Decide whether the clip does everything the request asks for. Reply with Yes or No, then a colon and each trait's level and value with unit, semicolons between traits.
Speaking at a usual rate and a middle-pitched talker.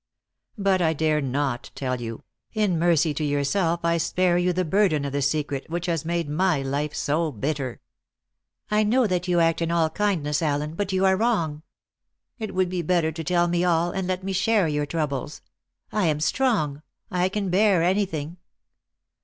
Yes: average, 185 wpm; medium, 170 Hz